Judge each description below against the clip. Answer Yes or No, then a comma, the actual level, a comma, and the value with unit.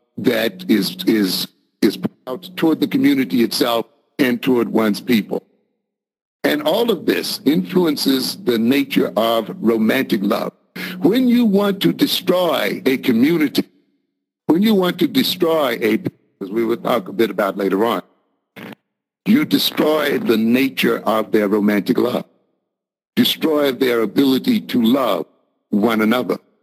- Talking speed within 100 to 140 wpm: Yes, slow, 135 wpm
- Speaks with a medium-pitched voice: Yes, medium, 155 Hz